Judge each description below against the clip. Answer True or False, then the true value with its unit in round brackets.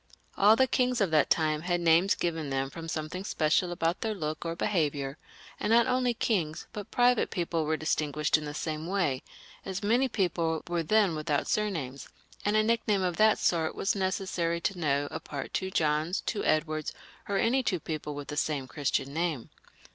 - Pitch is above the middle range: False (170 Hz)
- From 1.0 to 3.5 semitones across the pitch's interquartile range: False (4.7 semitones)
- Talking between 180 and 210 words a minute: True (185 wpm)